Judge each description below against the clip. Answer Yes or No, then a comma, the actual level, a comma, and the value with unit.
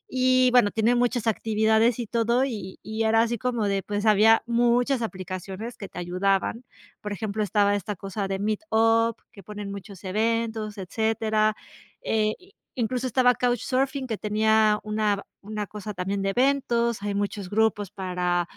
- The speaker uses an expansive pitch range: No, narrow, 2.5 semitones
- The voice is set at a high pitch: Yes, high, 215 Hz